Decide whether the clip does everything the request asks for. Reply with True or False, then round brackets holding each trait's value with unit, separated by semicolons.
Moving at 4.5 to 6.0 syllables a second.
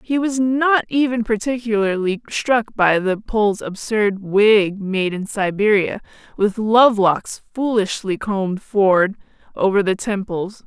False (4.0 syllables/s)